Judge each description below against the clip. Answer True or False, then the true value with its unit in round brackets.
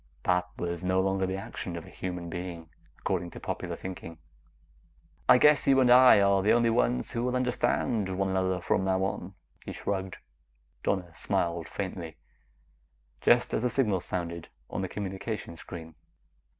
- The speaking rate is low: False (165 wpm)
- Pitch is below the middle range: True (95 Hz)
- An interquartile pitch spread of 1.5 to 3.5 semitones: True (2.8 semitones)